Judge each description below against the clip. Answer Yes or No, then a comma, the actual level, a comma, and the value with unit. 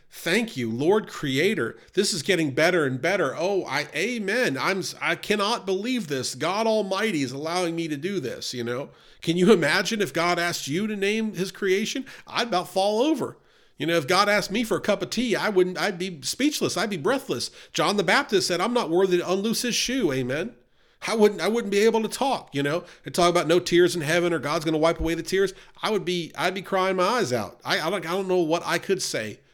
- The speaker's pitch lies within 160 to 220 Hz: Yes, medium, 185 Hz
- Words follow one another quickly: Yes, fast, 240 wpm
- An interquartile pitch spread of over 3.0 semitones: Yes, average, 3.6 semitones